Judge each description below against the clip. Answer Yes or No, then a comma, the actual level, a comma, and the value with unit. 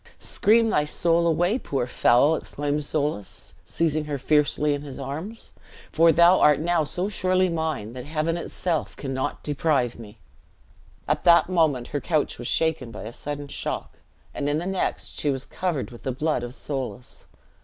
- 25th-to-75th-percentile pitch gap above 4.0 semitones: No, average, 3.7 semitones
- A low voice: No, medium, 150 Hz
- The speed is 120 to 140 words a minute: No, average, 170 wpm